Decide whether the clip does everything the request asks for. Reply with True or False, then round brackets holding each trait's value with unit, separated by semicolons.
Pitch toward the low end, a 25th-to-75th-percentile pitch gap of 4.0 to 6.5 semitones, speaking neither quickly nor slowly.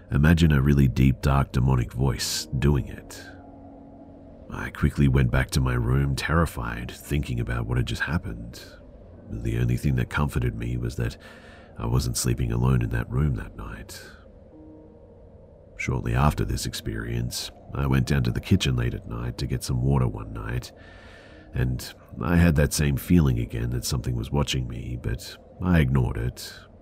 True (70 Hz; 5.5 semitones; 170 wpm)